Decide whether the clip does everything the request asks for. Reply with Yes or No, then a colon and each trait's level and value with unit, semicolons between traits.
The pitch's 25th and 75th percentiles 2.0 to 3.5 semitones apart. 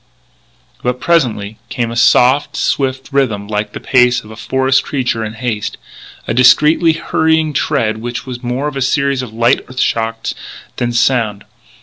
Yes: average, 3.2 semitones